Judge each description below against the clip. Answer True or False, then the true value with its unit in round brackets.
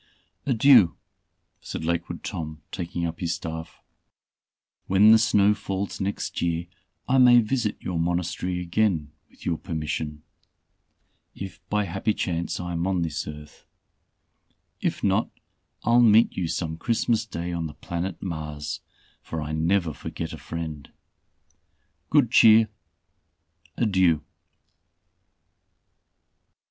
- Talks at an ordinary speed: False (120 wpm)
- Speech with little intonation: False (4.2 semitones)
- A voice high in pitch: False (85 Hz)